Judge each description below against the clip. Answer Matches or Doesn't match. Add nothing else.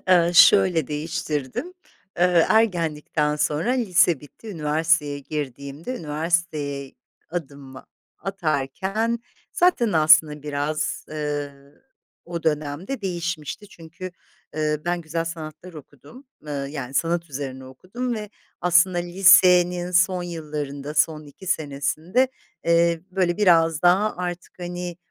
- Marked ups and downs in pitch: Doesn't match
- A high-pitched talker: Doesn't match